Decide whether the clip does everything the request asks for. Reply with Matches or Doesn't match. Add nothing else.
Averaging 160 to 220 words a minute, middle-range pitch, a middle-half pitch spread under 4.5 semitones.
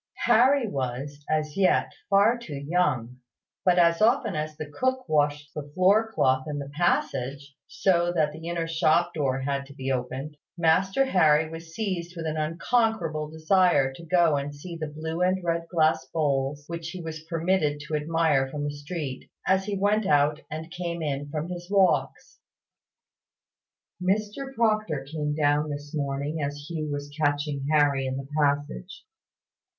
Matches